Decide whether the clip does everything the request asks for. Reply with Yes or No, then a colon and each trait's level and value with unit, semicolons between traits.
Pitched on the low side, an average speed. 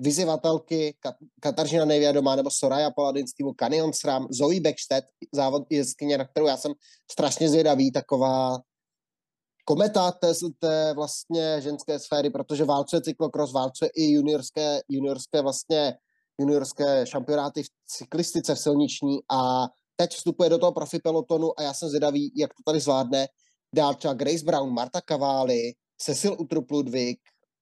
No: medium, 150 Hz; average, 140 wpm